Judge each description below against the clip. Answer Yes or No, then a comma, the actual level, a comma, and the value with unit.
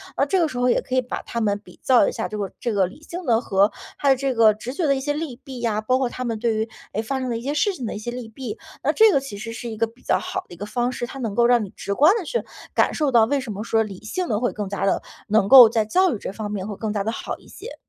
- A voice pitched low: No, high, 235 Hz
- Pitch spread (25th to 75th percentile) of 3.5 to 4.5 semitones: Yes, average, 3.9 semitones